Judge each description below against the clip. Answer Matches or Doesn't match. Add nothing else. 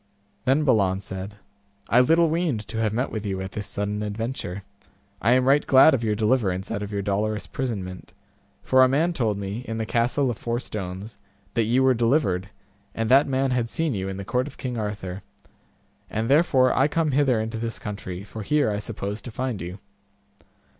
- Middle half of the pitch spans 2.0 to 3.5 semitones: Doesn't match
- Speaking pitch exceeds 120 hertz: Doesn't match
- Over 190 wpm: Matches